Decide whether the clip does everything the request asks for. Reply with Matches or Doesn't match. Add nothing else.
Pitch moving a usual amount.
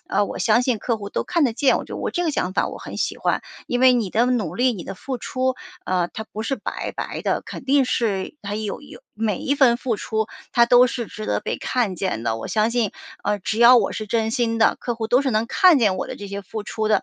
Matches